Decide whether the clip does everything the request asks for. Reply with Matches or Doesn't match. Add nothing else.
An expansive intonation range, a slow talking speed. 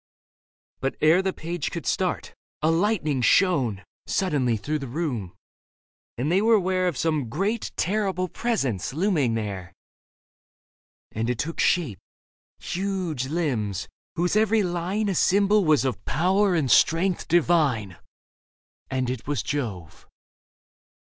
Matches